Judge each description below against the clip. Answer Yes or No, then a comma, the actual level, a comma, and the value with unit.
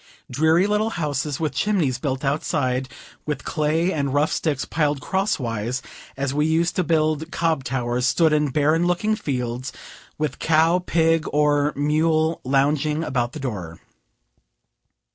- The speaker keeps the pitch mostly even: No, average, 3.3 semitones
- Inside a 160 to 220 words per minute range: No, average, 140 wpm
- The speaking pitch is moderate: Yes, medium, 150 Hz